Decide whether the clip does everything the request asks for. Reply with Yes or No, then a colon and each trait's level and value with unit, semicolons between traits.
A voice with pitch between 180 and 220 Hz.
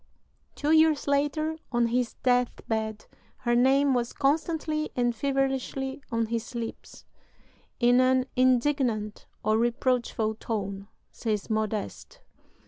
No: very high, 250 Hz